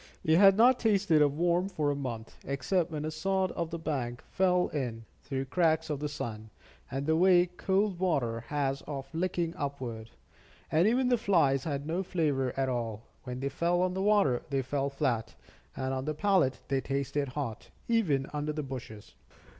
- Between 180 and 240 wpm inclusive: Yes, average, 185 wpm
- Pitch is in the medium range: Yes, medium, 150 Hz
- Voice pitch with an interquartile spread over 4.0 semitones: Yes, average, 5.1 semitones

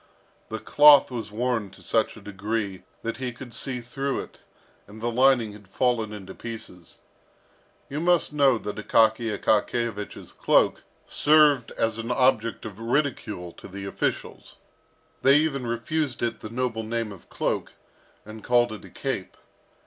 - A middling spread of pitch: Yes, average, 3.1 semitones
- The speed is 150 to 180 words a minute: Yes, average, 155 wpm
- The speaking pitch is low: Yes, low, 115 Hz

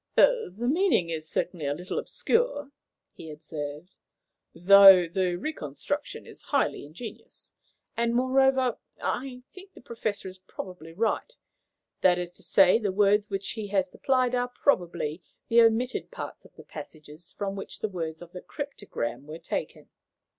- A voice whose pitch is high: Yes, high, 195 Hz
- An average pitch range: No, wide, 6.4 semitones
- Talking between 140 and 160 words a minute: Yes, average, 150 wpm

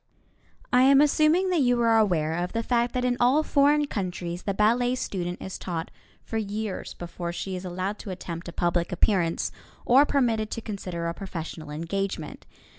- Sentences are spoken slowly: No, average, 180 wpm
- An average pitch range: No, wide, 5.9 semitones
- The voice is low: No, high, 200 Hz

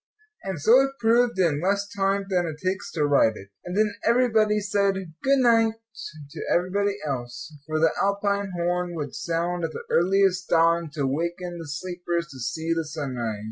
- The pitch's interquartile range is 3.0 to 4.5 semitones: Yes, average, 4.0 semitones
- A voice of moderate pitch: Yes, medium, 175 Hz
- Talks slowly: No, average, 180 wpm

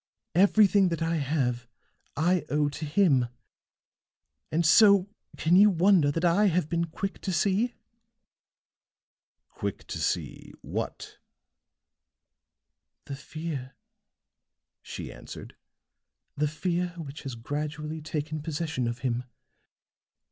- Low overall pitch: No, medium, 160 Hz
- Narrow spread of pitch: No, average, 3.8 semitones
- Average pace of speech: No, slow, 110 wpm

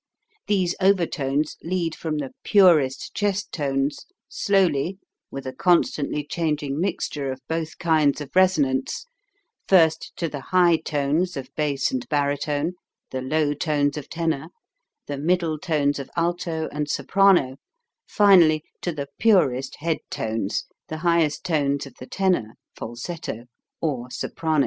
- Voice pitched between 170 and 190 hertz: No, medium, 155 Hz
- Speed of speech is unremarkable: No, slow, 130 wpm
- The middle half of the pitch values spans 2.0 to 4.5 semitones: Yes, average, 3.7 semitones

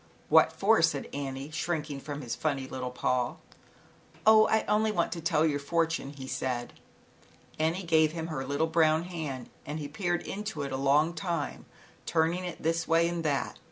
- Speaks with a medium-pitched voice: Yes, medium, 160 Hz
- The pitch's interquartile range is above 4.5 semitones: No, average, 3.3 semitones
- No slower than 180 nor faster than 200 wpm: Yes, average, 190 wpm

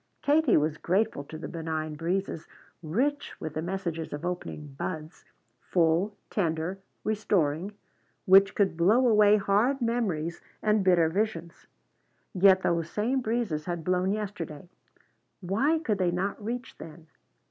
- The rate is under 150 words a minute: Yes, slow, 135 wpm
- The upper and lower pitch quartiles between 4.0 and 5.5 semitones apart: Yes, average, 4.7 semitones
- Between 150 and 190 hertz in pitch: Yes, medium, 185 Hz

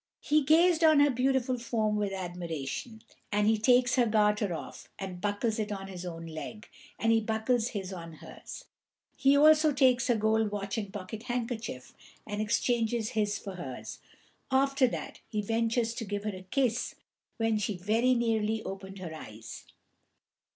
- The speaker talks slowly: No, average, 165 wpm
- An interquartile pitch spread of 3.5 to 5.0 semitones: Yes, average, 3.8 semitones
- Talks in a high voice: Yes, high, 220 Hz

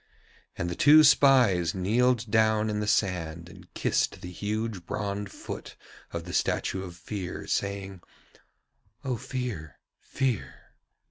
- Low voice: Yes, low, 100 Hz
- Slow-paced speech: Yes, slow, 130 wpm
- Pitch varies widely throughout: No, average, 4.3 semitones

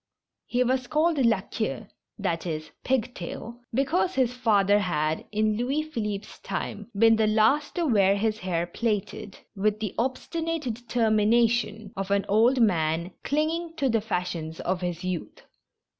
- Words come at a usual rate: Yes, average, 150 wpm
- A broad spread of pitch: No, average, 4.4 semitones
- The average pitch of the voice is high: Yes, high, 220 Hz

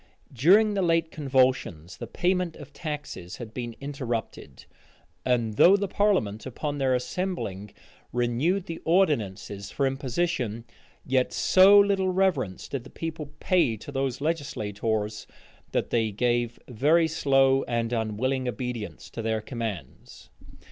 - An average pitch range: No, wide, 6.3 semitones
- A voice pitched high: No, low, 130 Hz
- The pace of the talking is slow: Yes, slow, 130 wpm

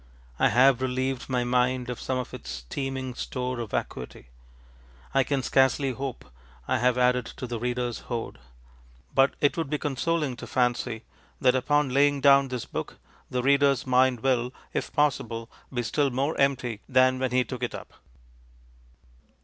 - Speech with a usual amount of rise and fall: No, narrow, 1.8 semitones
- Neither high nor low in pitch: No, low, 130 Hz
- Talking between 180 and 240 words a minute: No, average, 165 wpm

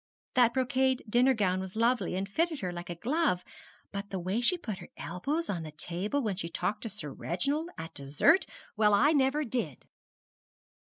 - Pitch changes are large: Yes, wide, 6.6 semitones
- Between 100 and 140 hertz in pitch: No, high, 210 Hz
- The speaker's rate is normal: Yes, average, 190 wpm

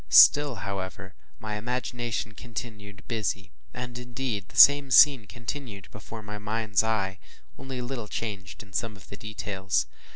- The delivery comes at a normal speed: Yes, average, 150 wpm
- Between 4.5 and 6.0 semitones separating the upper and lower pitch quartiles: No, average, 3.4 semitones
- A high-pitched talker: No, low, 110 Hz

